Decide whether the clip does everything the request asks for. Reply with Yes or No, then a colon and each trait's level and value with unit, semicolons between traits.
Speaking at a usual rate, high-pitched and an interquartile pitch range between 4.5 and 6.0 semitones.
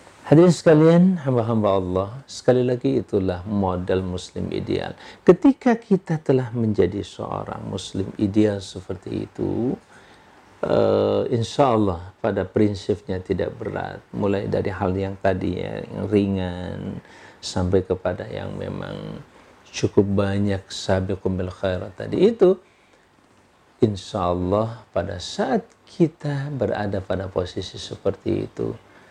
No: average, 110 wpm; low, 100 Hz; average, 4.9 semitones